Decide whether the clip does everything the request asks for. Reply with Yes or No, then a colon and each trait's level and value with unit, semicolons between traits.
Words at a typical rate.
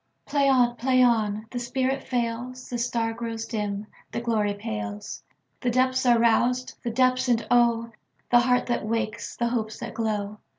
Yes: average, 145 wpm